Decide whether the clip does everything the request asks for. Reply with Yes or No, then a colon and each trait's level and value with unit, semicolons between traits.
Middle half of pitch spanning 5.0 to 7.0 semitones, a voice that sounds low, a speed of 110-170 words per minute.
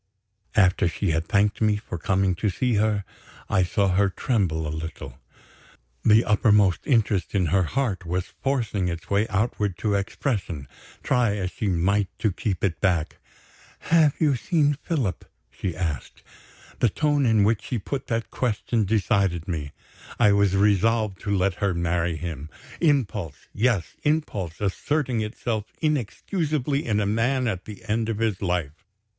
No: average, 4.2 semitones; low, 105 Hz; average, 155 wpm